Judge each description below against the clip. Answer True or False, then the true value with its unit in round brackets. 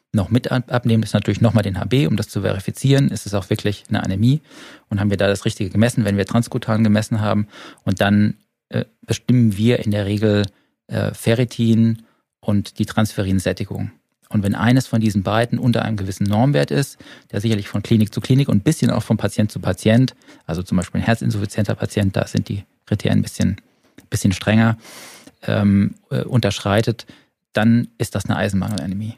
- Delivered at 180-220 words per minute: True (185 wpm)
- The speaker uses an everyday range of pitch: False (2.2 semitones)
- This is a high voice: False (110 Hz)